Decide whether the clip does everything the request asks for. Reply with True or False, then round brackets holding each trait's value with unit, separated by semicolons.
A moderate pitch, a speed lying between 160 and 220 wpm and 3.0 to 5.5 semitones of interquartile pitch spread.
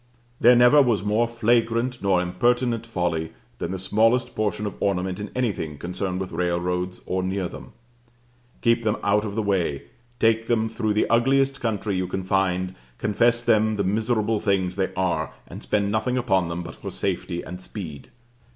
False (105 Hz; 175 wpm; 4.1 semitones)